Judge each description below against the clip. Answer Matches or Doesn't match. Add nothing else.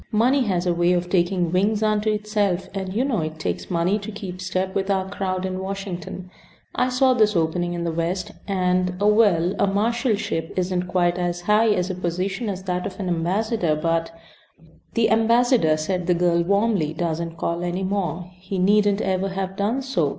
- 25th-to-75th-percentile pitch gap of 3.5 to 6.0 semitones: Doesn't match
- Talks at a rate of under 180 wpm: Doesn't match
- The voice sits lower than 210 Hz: Matches